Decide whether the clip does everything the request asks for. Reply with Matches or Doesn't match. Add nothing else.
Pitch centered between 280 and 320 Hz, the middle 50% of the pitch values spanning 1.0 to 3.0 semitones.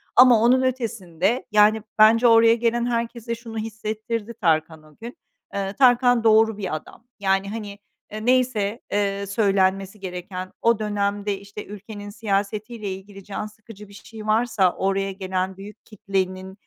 Doesn't match